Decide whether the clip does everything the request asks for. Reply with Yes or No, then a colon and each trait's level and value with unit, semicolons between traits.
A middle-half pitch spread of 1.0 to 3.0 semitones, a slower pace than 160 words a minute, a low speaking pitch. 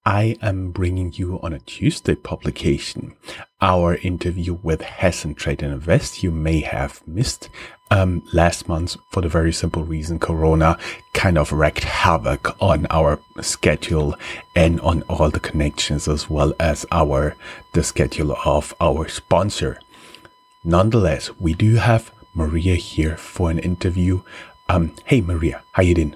Yes: narrow, 2.5 semitones; average, 145 wpm; very low, 85 Hz